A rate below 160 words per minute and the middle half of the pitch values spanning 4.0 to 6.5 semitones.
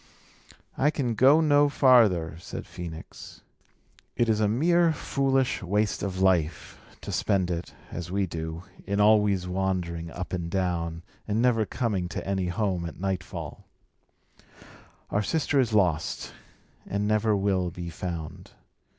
Yes: average, 140 wpm; average, 4.3 semitones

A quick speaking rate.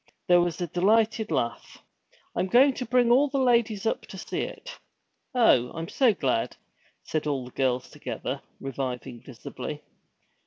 No: average, 155 wpm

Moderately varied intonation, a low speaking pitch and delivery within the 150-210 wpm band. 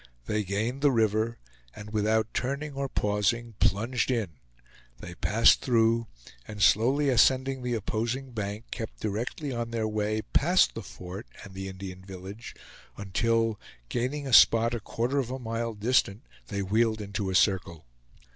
Yes: average, 3.0 semitones; low, 110 Hz; average, 155 wpm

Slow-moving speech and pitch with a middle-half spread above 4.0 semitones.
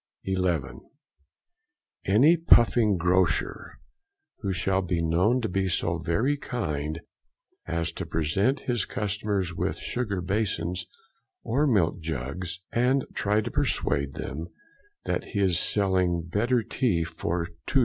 Yes: slow, 125 wpm; average, 4.5 semitones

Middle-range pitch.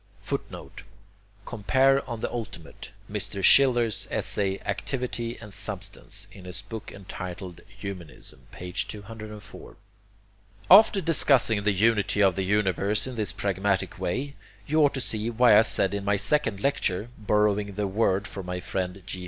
No: low, 105 Hz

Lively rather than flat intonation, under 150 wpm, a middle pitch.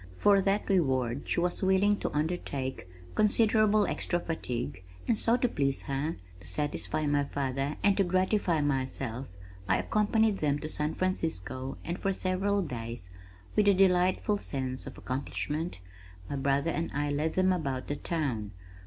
No: wide, 6.0 semitones; average, 155 wpm; medium, 155 Hz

